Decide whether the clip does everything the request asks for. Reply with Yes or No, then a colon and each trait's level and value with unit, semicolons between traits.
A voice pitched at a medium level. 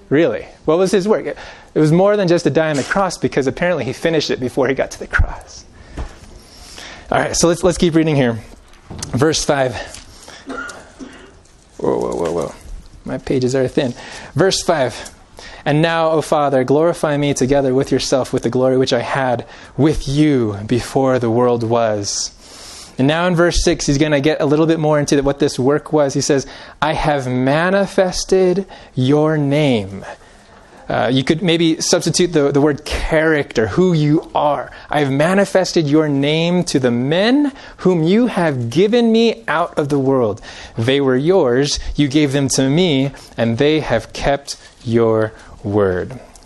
Yes: medium, 145 Hz